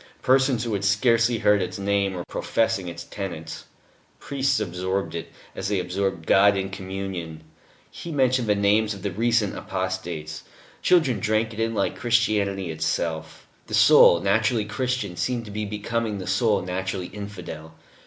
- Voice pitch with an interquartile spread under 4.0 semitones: Yes, average, 3.4 semitones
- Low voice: Yes, low, 100 Hz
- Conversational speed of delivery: Yes, average, 155 wpm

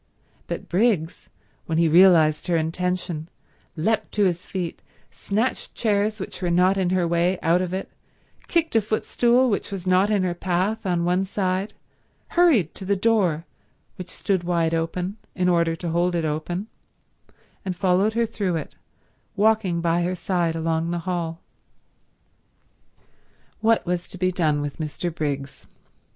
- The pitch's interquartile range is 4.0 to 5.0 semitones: No, average, 2.8 semitones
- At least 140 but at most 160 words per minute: Yes, average, 155 wpm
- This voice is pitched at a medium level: Yes, medium, 180 Hz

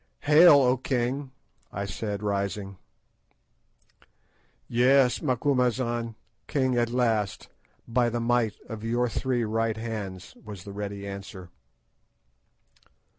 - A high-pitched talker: No, low, 115 Hz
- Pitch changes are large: No, average, 3.5 semitones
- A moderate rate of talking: No, slow, 105 wpm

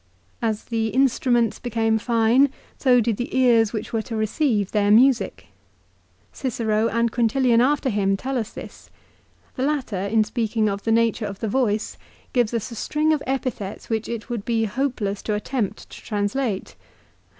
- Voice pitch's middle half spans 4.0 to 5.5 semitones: No, average, 2.8 semitones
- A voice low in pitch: No, high, 230 Hz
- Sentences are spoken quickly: No, average, 170 wpm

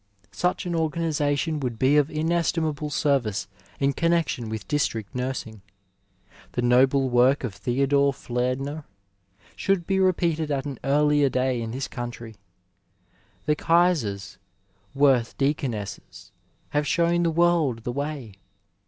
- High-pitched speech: No, medium, 140 Hz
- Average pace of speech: No, slow, 125 wpm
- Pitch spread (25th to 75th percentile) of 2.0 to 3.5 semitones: No, average, 4.4 semitones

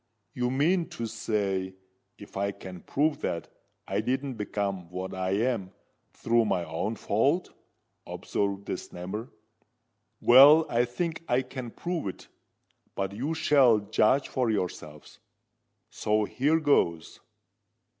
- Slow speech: Yes, slow, 125 wpm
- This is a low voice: Yes, low, 110 Hz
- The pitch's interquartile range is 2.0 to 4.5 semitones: No, wide, 5.5 semitones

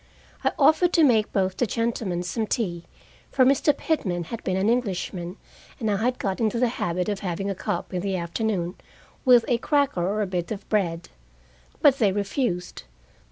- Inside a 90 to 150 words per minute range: No, average, 185 wpm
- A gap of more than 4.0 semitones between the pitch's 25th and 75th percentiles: Yes, average, 4.7 semitones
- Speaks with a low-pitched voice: No, high, 205 Hz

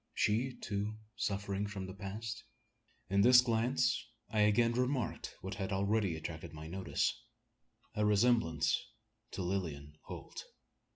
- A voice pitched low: Yes, low, 100 Hz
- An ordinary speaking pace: No, slow, 125 wpm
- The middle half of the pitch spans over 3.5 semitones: No, average, 3.2 semitones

